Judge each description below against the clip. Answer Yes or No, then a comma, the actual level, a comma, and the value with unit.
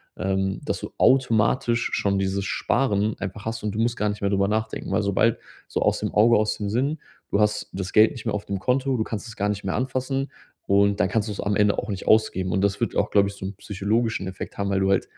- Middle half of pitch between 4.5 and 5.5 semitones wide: No, narrow, 2.4 semitones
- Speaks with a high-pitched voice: No, low, 105 Hz